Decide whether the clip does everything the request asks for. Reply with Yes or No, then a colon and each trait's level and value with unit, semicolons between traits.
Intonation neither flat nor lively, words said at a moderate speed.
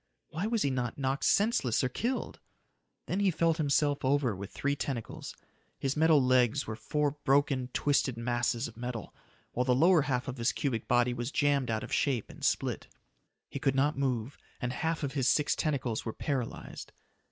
Yes: average, 3.2 semitones; average, 185 wpm